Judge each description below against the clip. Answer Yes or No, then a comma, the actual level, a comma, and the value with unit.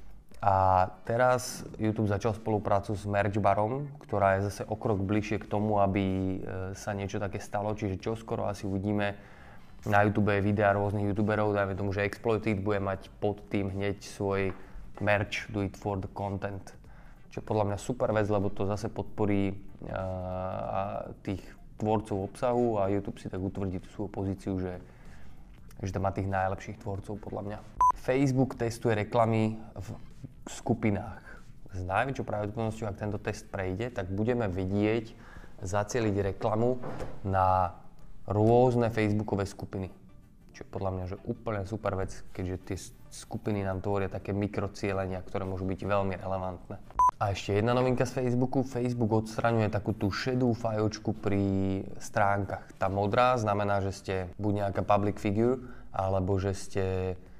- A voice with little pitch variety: Yes, narrow, 2.1 semitones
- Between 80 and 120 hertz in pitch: Yes, low, 100 Hz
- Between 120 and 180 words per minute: Yes, average, 150 wpm